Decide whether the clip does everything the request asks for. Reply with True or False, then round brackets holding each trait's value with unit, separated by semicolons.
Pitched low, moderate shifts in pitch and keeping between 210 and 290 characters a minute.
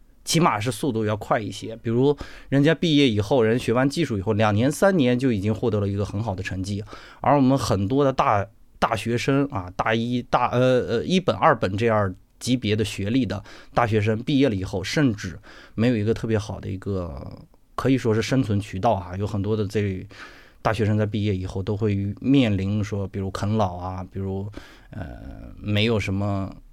True (110 Hz; 4.3 semitones; 285 characters per minute)